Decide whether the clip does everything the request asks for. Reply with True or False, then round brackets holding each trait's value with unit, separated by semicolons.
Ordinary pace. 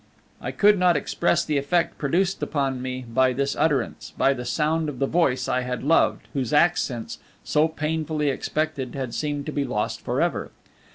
True (175 wpm)